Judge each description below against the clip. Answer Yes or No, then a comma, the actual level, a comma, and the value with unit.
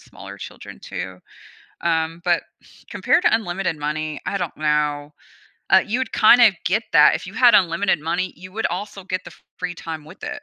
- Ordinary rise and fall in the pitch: Yes, average, 4.5 semitones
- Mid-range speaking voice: Yes, medium, 175 Hz